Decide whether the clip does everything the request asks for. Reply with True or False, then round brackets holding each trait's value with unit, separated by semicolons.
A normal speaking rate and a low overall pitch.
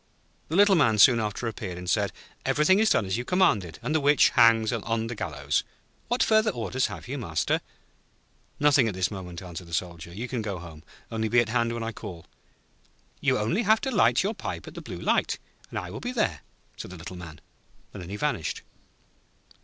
False (210 wpm; 115 Hz)